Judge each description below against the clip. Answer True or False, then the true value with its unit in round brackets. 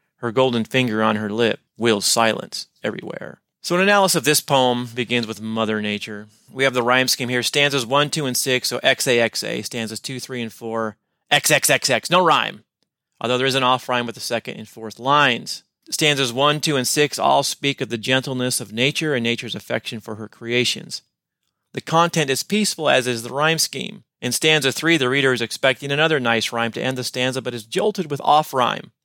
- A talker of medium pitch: False (125 Hz)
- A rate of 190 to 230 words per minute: True (205 wpm)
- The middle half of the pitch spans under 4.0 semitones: True (3.4 semitones)